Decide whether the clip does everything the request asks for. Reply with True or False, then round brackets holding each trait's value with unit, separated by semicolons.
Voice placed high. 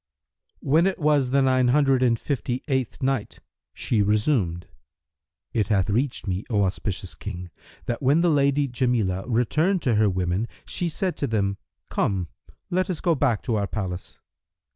False (120 Hz)